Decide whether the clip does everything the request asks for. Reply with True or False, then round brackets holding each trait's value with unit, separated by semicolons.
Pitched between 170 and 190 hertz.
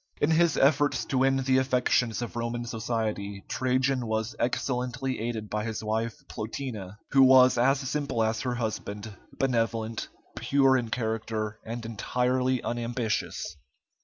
False (120 Hz)